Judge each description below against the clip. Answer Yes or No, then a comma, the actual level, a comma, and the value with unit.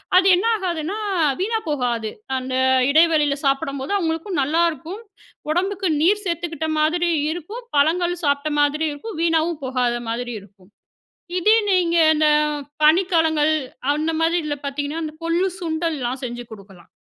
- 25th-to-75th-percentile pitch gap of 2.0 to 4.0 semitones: Yes, average, 3.7 semitones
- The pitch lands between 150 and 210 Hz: No, very high, 315 Hz